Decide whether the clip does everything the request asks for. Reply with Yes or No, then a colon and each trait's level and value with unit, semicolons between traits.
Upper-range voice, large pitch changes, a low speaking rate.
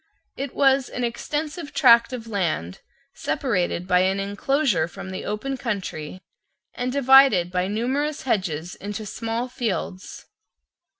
Yes: high, 225 Hz; wide, 6.1 semitones; slow, 125 wpm